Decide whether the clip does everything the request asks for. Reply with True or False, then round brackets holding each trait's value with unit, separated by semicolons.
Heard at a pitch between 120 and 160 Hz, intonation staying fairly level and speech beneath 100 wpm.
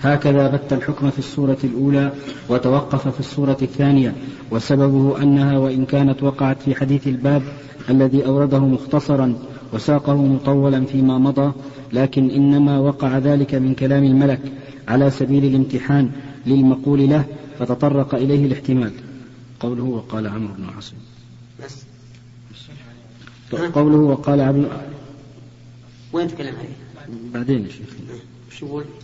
False (135 Hz; 1.8 semitones; 105 wpm)